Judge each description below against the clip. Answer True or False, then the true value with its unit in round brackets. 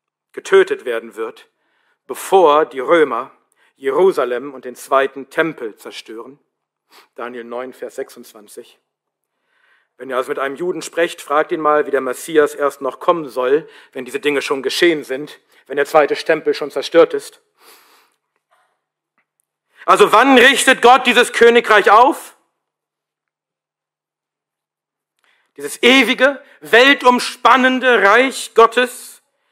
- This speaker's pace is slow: True (120 wpm)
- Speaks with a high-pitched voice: True (245 Hz)